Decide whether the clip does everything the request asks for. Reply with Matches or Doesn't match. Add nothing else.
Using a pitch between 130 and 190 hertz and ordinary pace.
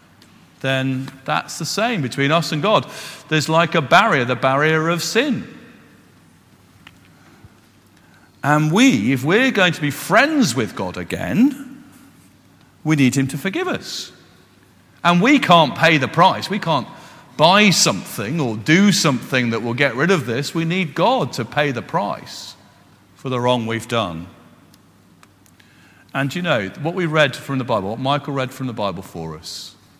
Matches